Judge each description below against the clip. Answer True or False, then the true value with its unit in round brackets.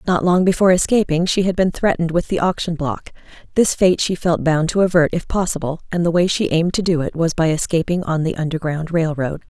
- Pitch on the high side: False (170 Hz)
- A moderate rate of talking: False (230 wpm)